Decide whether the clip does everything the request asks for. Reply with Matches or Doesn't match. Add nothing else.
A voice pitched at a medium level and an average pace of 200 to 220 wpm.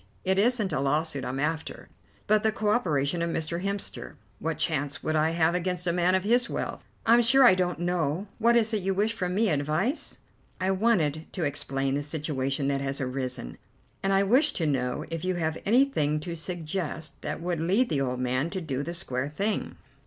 Matches